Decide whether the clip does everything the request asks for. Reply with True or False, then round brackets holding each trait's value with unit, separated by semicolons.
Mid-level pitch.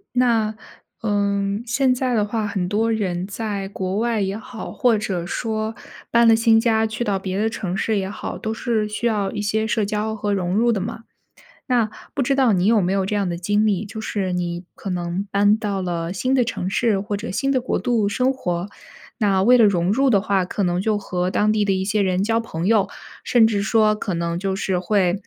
False (210 Hz)